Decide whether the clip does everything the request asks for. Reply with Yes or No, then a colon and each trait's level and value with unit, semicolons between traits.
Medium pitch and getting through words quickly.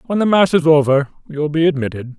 Yes: medium, 155 Hz; fast, 220 wpm